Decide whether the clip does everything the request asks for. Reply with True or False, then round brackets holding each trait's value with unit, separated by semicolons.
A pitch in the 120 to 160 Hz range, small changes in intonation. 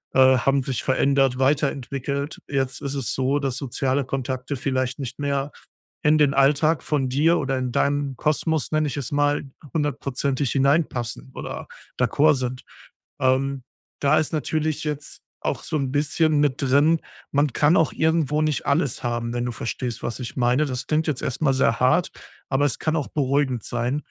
True (140 Hz; 2.3 semitones)